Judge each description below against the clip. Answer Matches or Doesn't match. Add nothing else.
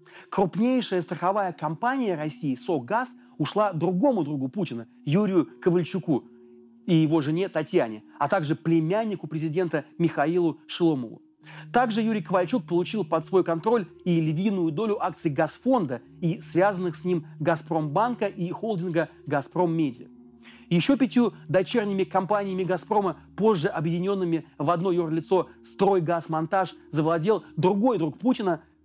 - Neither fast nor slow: Matches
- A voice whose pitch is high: Doesn't match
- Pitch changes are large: Doesn't match